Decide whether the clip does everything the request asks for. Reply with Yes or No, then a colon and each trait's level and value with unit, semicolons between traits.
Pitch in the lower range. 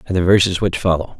Yes: very low, 90 Hz